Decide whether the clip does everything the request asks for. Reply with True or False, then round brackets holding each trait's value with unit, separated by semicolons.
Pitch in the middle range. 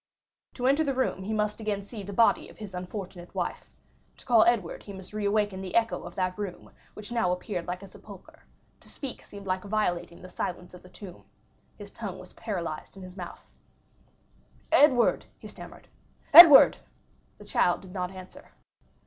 False (195 Hz)